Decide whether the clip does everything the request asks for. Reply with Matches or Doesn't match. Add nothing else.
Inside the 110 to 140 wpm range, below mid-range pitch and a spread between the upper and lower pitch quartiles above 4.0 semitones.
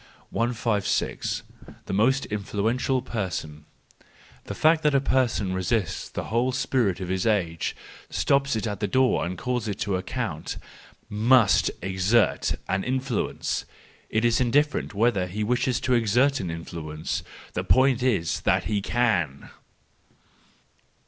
Matches